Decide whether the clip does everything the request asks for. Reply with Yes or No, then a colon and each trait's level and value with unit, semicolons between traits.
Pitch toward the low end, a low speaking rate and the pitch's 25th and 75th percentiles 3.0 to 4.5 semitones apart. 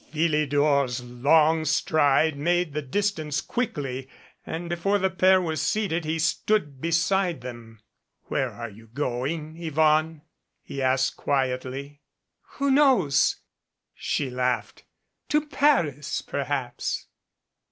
No: medium, 150 Hz; slow, 110 wpm; average, 4.2 semitones